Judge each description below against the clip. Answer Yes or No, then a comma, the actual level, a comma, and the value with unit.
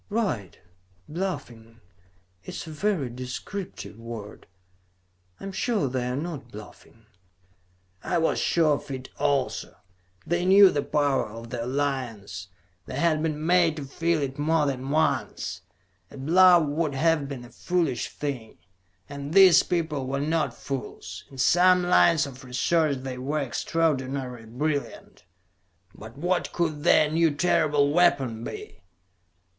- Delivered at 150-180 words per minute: No, average, 140 wpm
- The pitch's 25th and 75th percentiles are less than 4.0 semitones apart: No, average, 4.5 semitones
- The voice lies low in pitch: No, medium, 145 Hz